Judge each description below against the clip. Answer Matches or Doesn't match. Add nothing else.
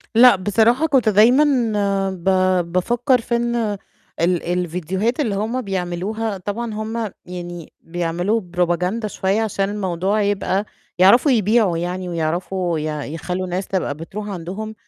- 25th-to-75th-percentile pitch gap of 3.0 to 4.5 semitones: Matches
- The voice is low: Doesn't match